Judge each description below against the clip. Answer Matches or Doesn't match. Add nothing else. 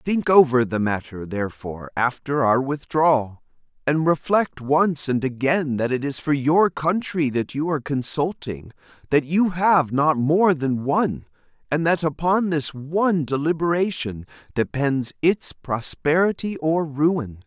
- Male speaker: Matches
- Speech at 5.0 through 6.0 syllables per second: Doesn't match